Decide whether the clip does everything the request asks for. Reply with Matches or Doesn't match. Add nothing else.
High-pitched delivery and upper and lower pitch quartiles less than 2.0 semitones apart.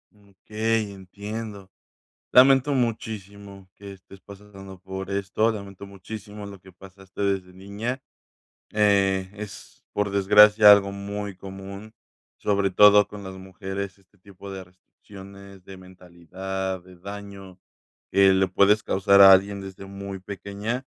Doesn't match